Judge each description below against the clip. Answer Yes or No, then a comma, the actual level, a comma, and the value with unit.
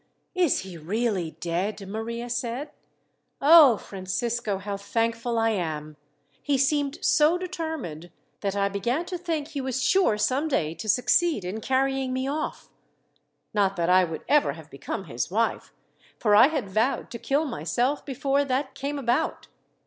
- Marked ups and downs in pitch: Yes, wide, 6.0 semitones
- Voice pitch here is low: No, high, 235 Hz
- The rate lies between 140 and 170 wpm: Yes, average, 155 wpm